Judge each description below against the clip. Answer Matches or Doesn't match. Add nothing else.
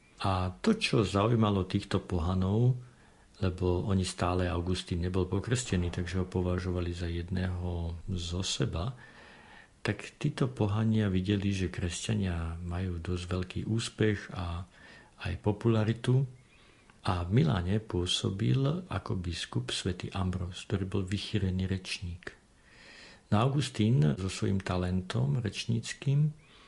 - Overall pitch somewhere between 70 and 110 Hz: Matches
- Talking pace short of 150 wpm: Matches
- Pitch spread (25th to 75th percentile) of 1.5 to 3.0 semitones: Doesn't match